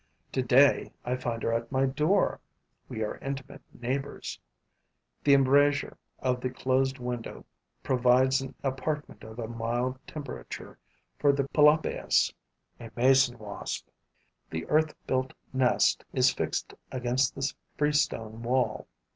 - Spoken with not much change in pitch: Yes, narrow, 2.3 semitones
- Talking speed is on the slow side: Yes, slow, 125 wpm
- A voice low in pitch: Yes, low, 130 Hz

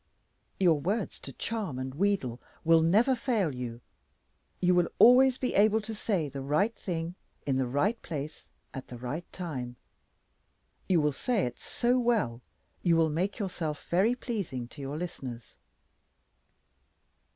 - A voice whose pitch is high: No, medium, 170 Hz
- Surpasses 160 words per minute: No, average, 150 wpm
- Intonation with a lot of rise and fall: Yes, wide, 7.5 semitones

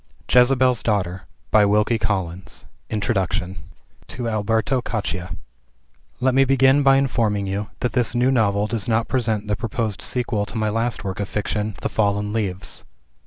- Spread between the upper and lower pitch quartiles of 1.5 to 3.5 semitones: Yes, average, 3.2 semitones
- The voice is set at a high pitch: No, low, 110 Hz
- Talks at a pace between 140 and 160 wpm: Yes, average, 150 wpm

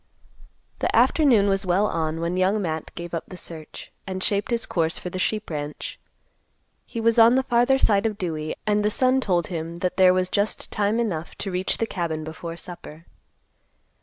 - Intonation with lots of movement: No, average, 4.2 semitones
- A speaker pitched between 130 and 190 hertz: Yes, medium, 185 Hz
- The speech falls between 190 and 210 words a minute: Yes, average, 195 wpm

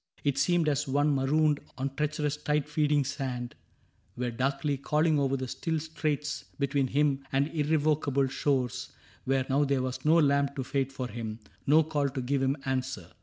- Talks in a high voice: No, medium, 140 Hz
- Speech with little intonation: Yes, narrow, 2.0 semitones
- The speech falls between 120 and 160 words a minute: No, average, 170 wpm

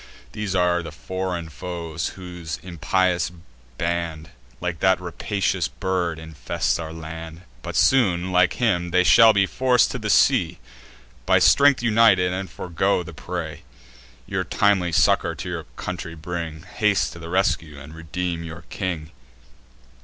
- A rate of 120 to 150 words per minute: Yes, average, 140 wpm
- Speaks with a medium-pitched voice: No, very low, 90 Hz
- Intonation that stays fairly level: Yes, narrow, 2.3 semitones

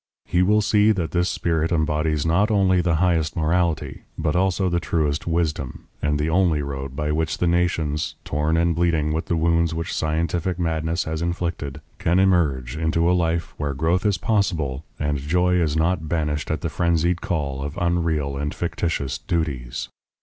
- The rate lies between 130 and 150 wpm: No, average, 175 wpm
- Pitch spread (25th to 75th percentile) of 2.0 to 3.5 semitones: Yes, narrow, 2.5 semitones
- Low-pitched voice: Yes, very low, 80 Hz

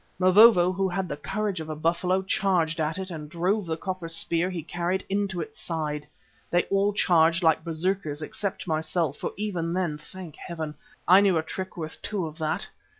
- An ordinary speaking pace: Yes, average, 190 wpm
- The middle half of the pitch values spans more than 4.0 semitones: No, average, 3.0 semitones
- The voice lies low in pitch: No, medium, 175 Hz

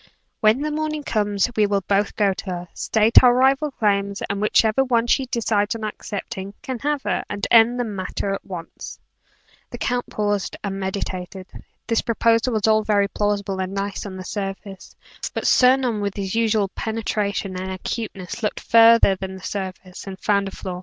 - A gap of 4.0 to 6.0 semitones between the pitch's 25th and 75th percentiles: No, average, 2.8 semitones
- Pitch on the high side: Yes, high, 205 Hz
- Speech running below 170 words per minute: No, average, 185 wpm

